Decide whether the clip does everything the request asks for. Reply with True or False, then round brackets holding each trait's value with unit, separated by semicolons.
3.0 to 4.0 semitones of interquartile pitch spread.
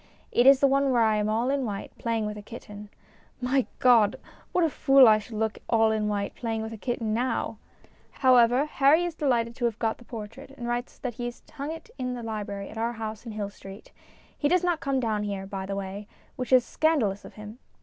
True (3.5 semitones)